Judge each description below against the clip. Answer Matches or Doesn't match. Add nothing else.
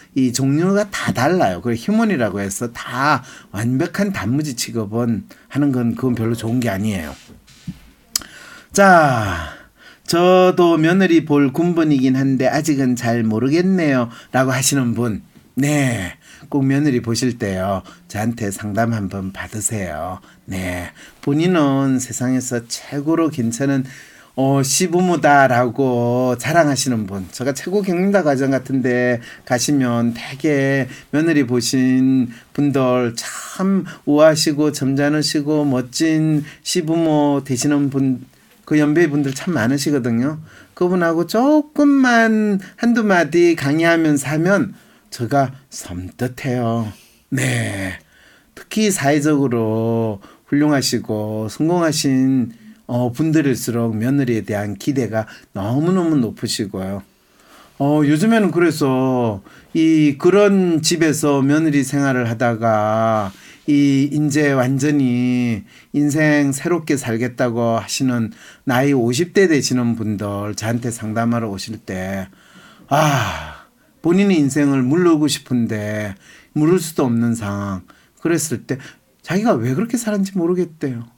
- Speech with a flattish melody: Doesn't match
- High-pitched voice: Doesn't match